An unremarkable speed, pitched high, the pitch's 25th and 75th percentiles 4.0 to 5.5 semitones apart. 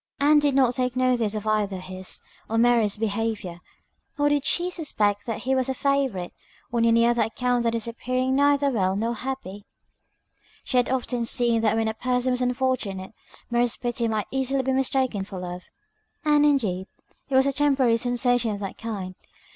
No: average, 180 wpm; high, 240 Hz; average, 3.5 semitones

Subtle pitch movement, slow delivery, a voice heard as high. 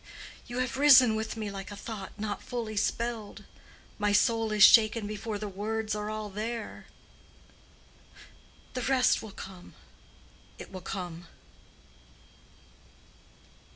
Yes: narrow, 2.1 semitones; slow, 120 wpm; high, 215 Hz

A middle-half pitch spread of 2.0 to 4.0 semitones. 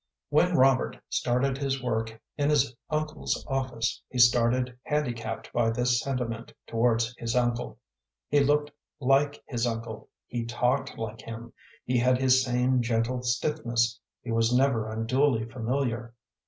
Yes: narrow, 2.5 semitones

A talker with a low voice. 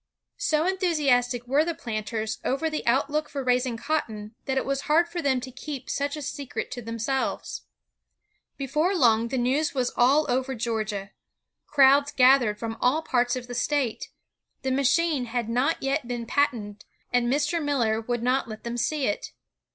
No: very high, 260 Hz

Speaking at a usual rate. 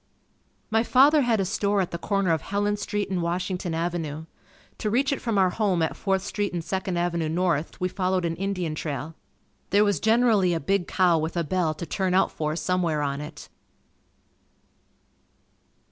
Yes: average, 180 wpm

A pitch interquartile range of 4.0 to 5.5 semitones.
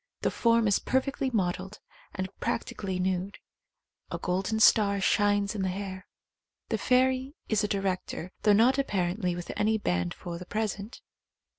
No: average, 2.9 semitones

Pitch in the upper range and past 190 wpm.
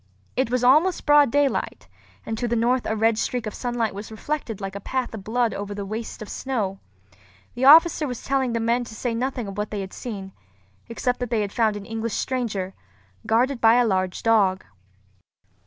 Yes: high, 230 Hz; average, 200 wpm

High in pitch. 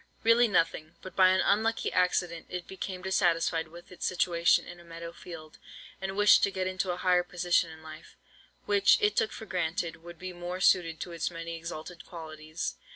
No: medium, 175 Hz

